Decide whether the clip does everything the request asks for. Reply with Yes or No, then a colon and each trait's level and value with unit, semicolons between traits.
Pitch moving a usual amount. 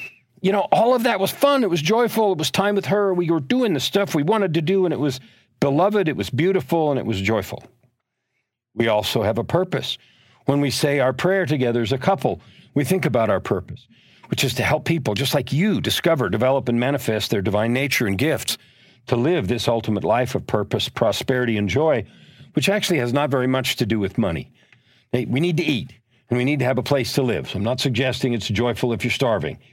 No: wide, 6.0 semitones